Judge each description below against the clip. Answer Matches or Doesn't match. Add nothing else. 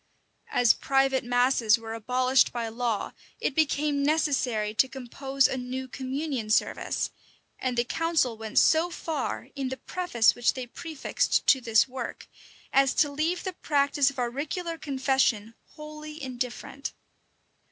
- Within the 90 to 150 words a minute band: Matches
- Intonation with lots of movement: Doesn't match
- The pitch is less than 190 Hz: Doesn't match